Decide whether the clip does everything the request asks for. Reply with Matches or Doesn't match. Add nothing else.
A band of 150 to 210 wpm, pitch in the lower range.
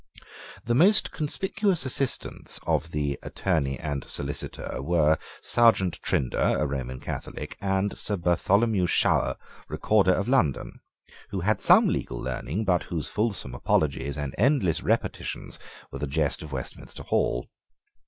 Doesn't match